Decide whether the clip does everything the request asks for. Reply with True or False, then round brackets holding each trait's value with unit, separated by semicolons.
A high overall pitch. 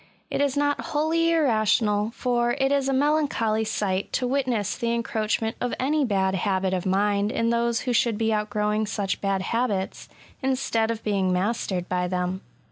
True (220 Hz)